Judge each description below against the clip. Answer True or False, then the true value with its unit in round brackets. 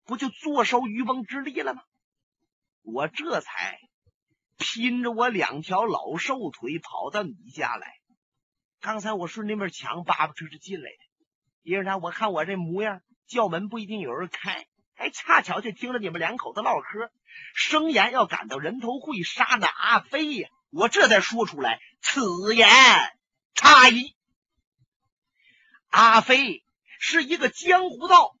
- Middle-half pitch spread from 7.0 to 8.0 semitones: False (5.1 semitones)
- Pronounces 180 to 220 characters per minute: True (215 characters per minute)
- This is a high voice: True (240 Hz)